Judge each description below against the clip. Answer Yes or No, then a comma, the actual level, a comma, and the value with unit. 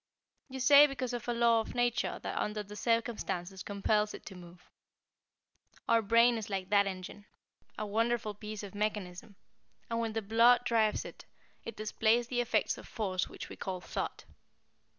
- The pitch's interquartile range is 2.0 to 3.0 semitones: Yes, narrow, 2.6 semitones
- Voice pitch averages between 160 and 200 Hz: No, high, 215 Hz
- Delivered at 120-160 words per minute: No, average, 170 wpm